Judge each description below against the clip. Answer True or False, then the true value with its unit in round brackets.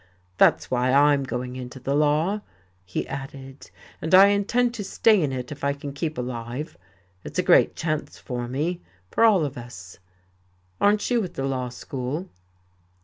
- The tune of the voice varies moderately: False (5.7 semitones)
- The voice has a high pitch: False (140 Hz)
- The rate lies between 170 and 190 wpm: True (175 wpm)